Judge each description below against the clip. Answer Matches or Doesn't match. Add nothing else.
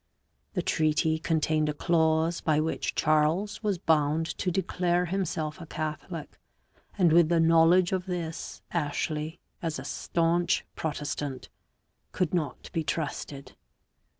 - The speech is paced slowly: Matches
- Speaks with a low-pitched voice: Doesn't match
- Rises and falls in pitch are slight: Matches